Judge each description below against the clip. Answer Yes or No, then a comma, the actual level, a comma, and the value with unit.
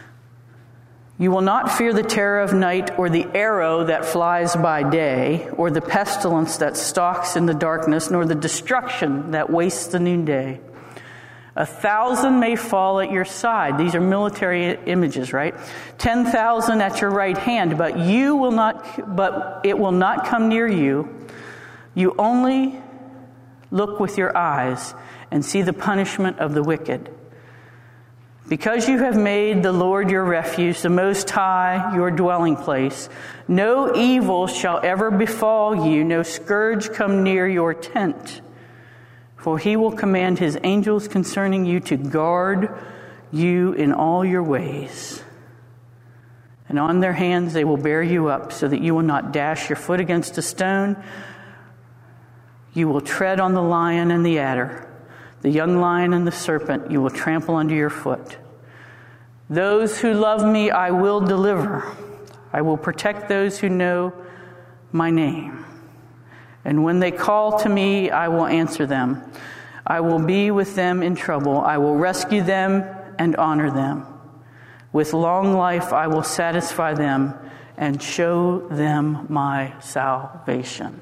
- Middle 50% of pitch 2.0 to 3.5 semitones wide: No, average, 4.9 semitones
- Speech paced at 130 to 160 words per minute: Yes, average, 150 wpm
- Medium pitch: Yes, medium, 170 Hz